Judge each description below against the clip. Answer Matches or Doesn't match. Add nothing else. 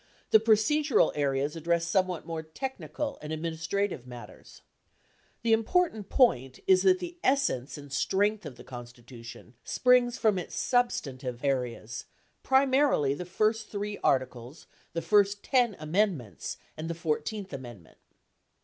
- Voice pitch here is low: Doesn't match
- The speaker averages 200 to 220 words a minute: Doesn't match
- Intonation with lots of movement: Matches